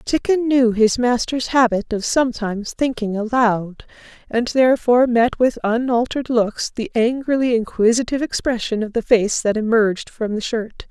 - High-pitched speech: Yes, high, 235 Hz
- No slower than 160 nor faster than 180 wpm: No, average, 150 wpm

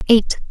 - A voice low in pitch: No, high, 225 Hz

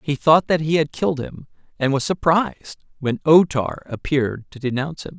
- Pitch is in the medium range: Yes, medium, 150 Hz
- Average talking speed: Yes, average, 195 wpm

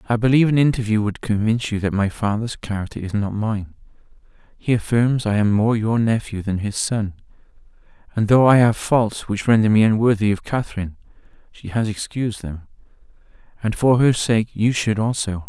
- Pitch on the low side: Yes, low, 110 Hz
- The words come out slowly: No, average, 180 wpm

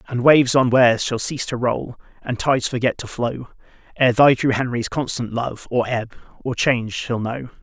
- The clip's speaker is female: No, male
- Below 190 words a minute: No, average, 195 wpm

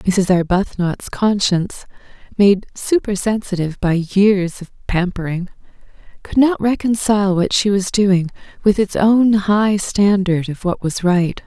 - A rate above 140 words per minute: No, slow, 135 wpm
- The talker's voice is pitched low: No, high, 195 Hz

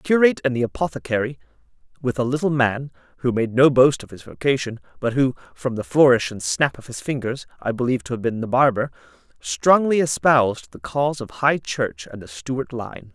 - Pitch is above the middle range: No, low, 130 Hz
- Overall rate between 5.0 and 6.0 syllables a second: Yes, 5.5 syllables/s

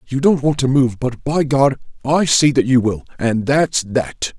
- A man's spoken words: Yes, male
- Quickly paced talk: Yes, fast, 220 wpm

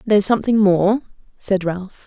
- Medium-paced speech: Yes, average, 145 wpm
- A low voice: No, high, 200 Hz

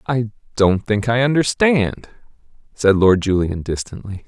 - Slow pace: Yes, slow, 125 wpm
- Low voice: Yes, low, 110 Hz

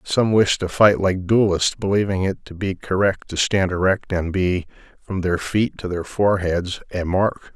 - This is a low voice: Yes, very low, 95 Hz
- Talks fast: No, average, 190 wpm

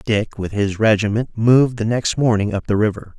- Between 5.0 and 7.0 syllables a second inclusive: Yes, 5.3 syllables/s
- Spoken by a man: Yes, male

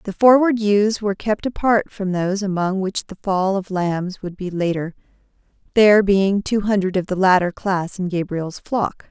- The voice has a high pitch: Yes, high, 195 Hz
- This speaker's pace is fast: No, average, 185 wpm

